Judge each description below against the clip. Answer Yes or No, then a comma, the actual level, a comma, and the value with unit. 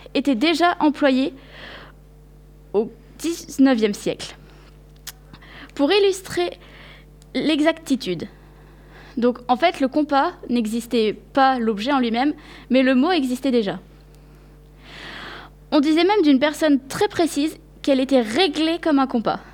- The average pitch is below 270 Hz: No, very high, 275 Hz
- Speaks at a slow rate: Yes, slow, 115 wpm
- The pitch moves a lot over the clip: No, average, 4.3 semitones